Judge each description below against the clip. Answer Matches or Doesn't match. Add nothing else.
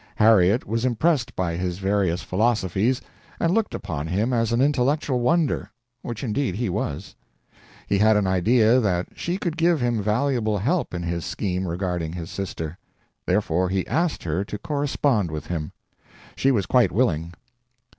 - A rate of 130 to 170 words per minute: Matches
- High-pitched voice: Doesn't match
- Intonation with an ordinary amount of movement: Doesn't match